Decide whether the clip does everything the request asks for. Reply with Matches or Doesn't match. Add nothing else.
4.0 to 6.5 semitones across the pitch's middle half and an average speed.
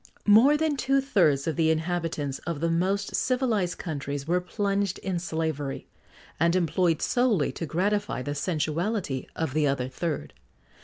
Matches